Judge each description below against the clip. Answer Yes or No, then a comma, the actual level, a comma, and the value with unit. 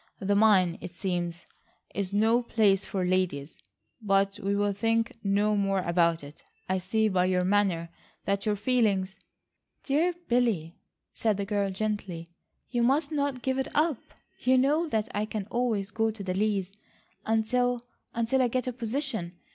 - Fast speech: No, average, 160 wpm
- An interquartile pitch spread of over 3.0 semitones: Yes, average, 4.0 semitones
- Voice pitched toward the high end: Yes, high, 205 Hz